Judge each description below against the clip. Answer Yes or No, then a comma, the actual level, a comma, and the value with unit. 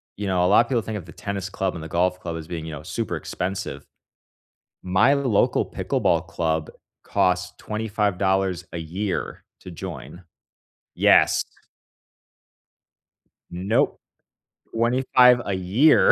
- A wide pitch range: No, average, 3.5 semitones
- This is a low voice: Yes, very low, 95 Hz